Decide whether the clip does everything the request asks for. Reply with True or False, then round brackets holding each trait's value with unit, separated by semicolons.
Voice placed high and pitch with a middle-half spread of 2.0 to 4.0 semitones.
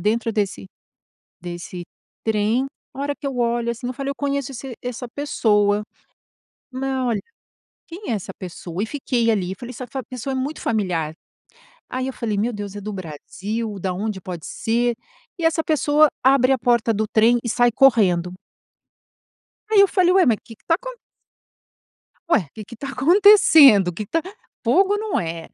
False (235 Hz; 4.8 semitones)